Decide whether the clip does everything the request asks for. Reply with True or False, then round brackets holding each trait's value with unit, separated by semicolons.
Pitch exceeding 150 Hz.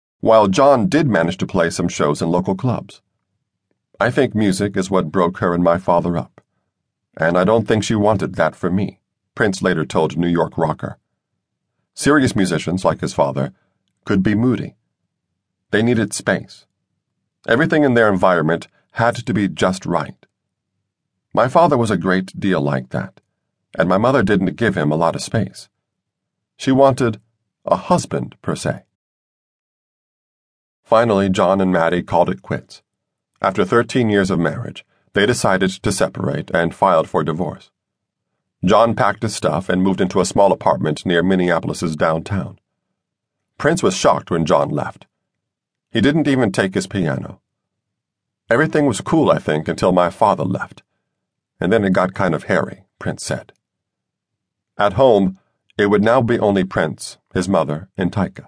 False (95 Hz)